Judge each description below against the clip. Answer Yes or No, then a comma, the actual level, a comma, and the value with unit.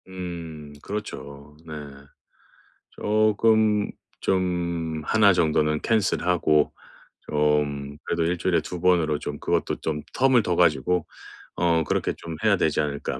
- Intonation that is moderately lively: Yes, average, 3.7 semitones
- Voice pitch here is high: No, very low, 85 Hz